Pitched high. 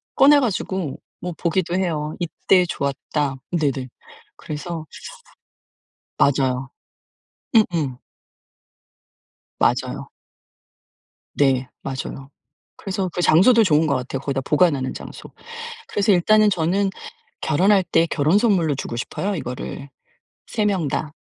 No: medium, 160 Hz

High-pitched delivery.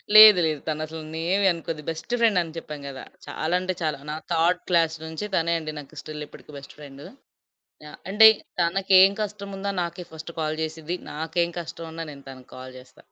No: medium, 165 Hz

